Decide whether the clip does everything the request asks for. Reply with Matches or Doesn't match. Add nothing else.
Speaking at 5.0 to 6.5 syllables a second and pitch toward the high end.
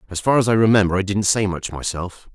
Doesn't match